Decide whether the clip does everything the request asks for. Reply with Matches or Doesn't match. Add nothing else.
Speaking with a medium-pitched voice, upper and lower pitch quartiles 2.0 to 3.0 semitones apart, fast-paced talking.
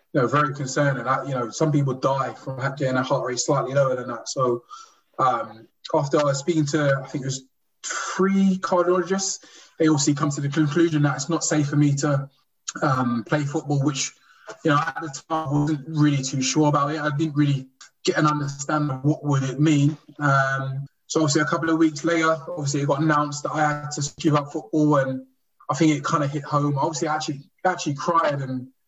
Matches